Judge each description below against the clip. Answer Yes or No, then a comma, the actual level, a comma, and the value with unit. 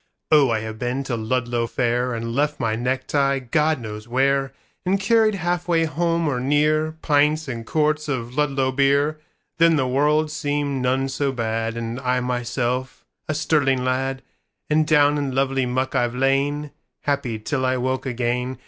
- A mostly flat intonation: No, average, 3.2 semitones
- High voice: No, low, 135 Hz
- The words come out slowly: No, average, 145 wpm